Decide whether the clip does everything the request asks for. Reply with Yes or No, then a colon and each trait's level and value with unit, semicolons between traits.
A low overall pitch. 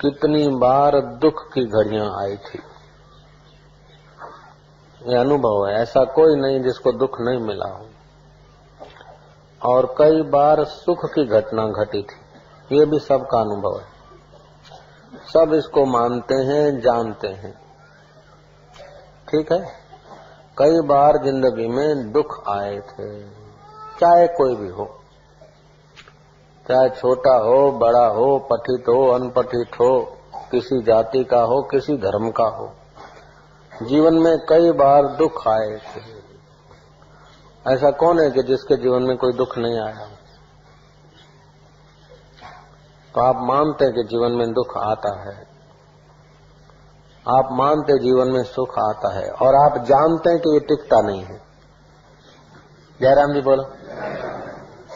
Yes: low, 130 Hz